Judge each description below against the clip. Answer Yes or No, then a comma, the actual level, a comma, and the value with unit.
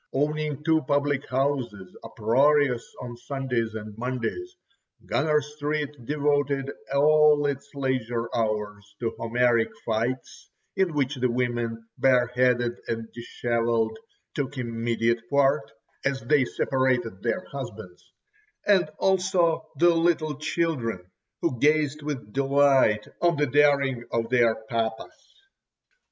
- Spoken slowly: Yes, slow, 115 wpm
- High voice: No, low, 130 Hz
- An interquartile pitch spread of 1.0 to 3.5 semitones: No, average, 4.0 semitones